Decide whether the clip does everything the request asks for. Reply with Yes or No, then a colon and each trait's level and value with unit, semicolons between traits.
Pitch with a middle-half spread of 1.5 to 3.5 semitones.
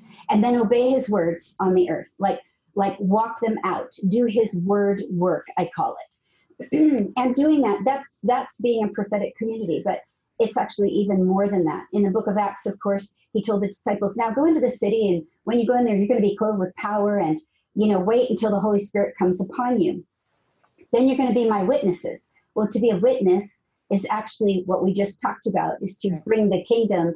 Yes: average, 3.2 semitones